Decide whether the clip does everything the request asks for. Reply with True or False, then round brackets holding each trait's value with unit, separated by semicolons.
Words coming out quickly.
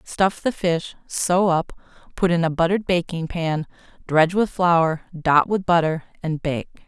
False (165 wpm)